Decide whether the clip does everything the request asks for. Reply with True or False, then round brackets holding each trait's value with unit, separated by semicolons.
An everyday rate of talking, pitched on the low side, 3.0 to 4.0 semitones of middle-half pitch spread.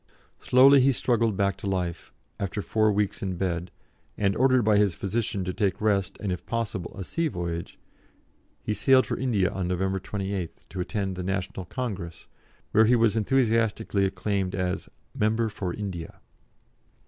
True (160 wpm; 100 Hz; 3.3 semitones)